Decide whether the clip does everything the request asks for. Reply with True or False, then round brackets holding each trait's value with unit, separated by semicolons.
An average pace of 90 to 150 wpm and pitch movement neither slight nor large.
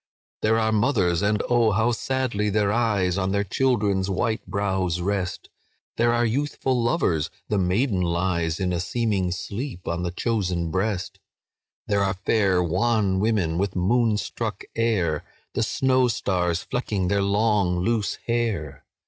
True (140 wpm; 4.0 semitones)